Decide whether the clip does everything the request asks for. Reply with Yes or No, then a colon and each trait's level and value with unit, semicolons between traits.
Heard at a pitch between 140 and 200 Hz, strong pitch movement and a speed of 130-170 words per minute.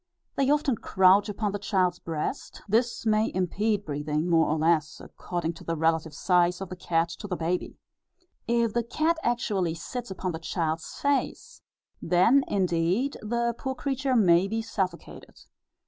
Yes: high, 190 Hz; wide, 5.7 semitones; average, 160 wpm